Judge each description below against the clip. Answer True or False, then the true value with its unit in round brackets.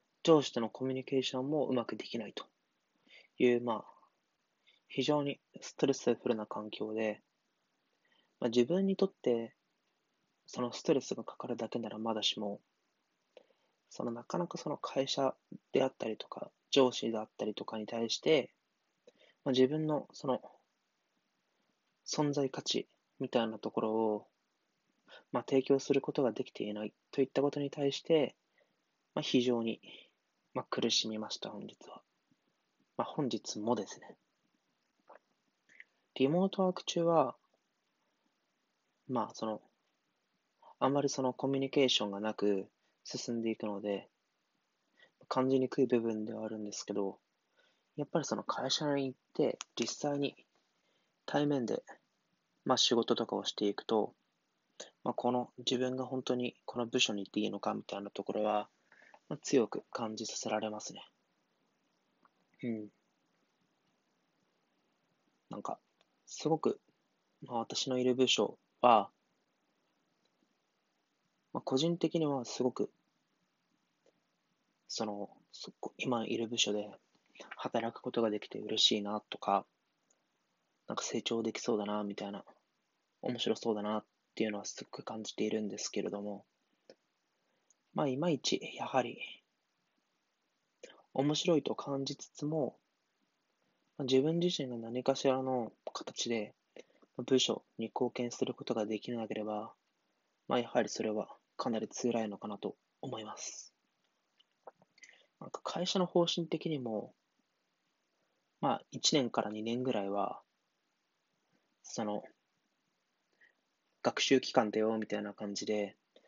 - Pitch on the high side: False (120 Hz)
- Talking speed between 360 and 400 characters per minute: False (245 characters per minute)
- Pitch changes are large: False (4.0 semitones)